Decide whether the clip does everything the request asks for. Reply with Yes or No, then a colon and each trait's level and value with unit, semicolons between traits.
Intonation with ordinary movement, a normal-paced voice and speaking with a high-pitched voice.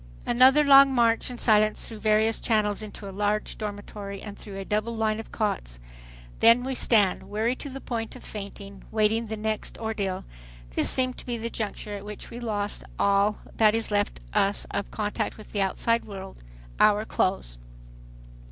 No: narrow, 2.1 semitones; average, 175 wpm; high, 215 Hz